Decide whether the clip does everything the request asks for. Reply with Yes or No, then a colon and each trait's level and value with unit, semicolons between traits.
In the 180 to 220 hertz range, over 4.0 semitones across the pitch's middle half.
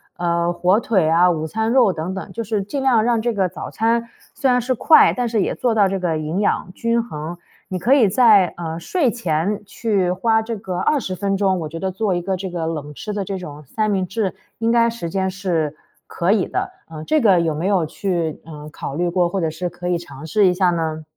Yes: high, 190 Hz; average, 4.6 semitones